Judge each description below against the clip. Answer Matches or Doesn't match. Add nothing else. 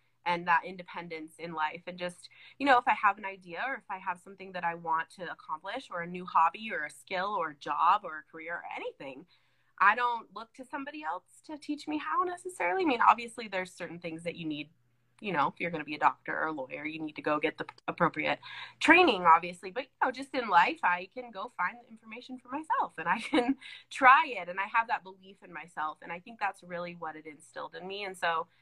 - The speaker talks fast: Matches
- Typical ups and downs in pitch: Doesn't match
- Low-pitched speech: Doesn't match